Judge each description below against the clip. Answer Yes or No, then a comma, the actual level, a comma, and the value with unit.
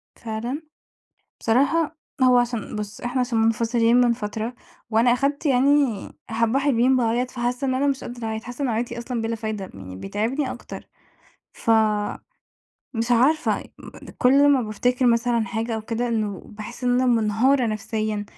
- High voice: Yes, high, 240 Hz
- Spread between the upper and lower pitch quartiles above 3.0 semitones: No, narrow, 2.4 semitones